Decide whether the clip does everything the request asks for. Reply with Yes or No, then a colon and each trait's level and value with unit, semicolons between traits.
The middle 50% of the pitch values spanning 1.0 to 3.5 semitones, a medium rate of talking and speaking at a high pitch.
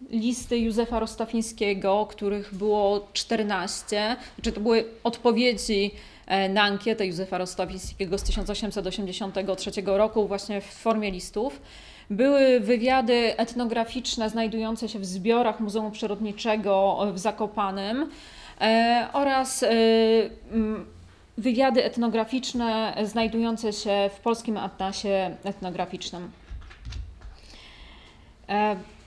No: narrow, 2.6 semitones; slow, 85 wpm; high, 215 Hz